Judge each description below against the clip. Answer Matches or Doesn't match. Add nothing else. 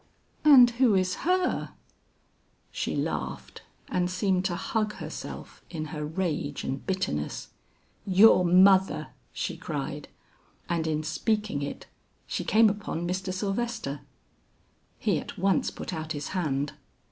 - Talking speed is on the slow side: Matches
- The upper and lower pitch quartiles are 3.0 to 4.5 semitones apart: Doesn't match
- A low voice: Doesn't match